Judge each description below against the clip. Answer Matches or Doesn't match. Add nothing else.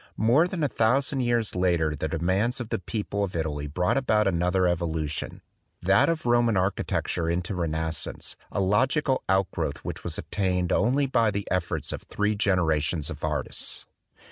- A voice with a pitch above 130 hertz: Doesn't match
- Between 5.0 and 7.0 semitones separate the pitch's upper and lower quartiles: Matches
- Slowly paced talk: Doesn't match